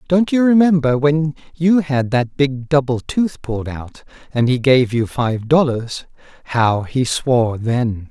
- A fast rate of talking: No, average, 165 wpm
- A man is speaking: Yes, male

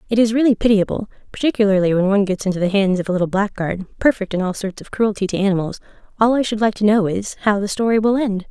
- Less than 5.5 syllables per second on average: No, 6.8 syllables/s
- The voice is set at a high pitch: Yes, high, 205 Hz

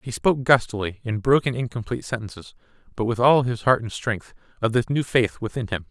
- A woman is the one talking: No, male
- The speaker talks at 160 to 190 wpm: No, fast, 205 wpm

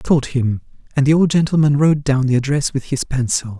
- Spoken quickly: Yes, fast, 235 wpm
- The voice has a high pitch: No, medium, 140 Hz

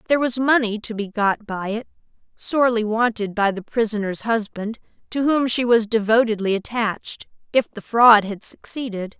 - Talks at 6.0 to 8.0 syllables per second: No, 2.8 syllables/s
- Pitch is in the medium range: No, high, 225 Hz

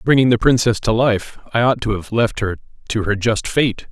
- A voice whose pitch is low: Yes, low, 115 Hz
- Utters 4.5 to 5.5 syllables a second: Yes, 5.1 syllables/s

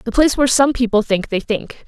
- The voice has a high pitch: Yes, high, 240 Hz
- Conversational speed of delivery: No, fast, 255 wpm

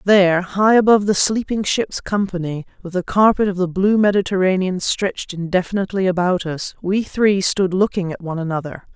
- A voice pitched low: No, high, 190 Hz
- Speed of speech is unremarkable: Yes, average, 170 wpm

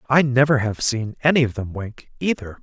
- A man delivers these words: Yes, male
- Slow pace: No, fast, 205 wpm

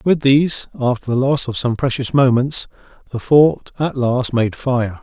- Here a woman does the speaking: No, male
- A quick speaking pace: No, average, 180 wpm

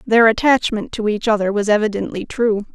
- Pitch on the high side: Yes, high, 215 Hz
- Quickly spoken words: No, average, 175 wpm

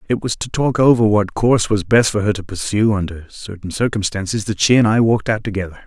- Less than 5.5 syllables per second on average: No, 6.0 syllables/s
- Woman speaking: No, male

